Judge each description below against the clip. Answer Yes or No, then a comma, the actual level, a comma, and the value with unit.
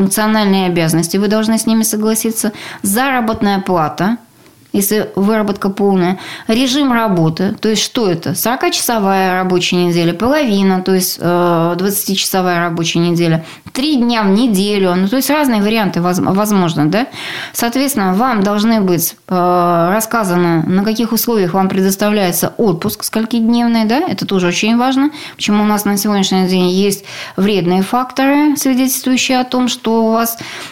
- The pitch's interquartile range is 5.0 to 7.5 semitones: No, average, 3.9 semitones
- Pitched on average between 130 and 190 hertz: No, high, 205 Hz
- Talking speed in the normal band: Yes, average, 140 wpm